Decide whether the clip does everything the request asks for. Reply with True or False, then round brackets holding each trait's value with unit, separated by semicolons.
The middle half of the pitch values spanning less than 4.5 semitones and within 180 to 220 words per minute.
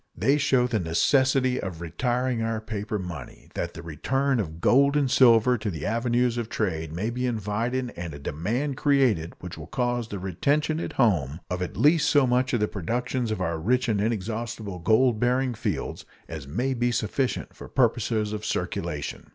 False (4.9 semitones; 185 wpm)